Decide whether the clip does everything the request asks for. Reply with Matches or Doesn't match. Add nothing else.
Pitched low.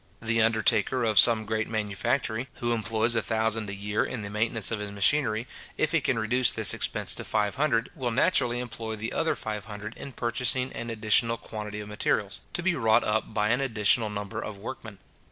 Matches